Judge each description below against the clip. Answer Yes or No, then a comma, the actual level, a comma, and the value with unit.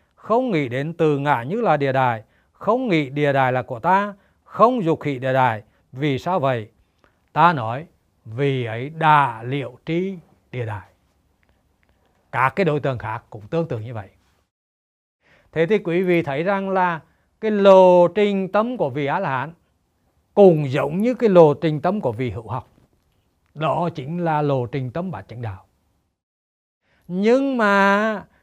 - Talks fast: No, average, 170 wpm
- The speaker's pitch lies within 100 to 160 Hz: Yes, medium, 140 Hz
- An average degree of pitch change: No, wide, 8.4 semitones